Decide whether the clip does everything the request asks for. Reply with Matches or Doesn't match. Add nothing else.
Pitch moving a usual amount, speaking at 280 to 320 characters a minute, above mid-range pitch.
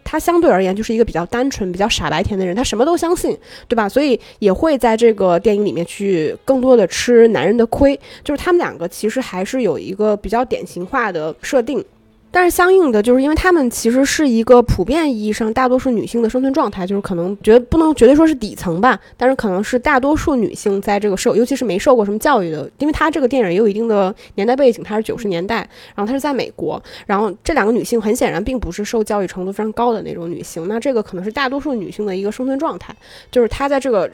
Doesn't match